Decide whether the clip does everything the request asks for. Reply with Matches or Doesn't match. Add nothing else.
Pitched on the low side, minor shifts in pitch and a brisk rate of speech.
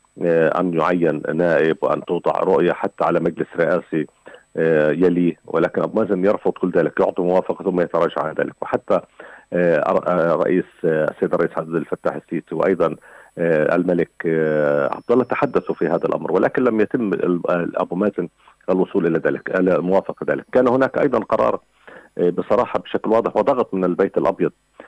Matches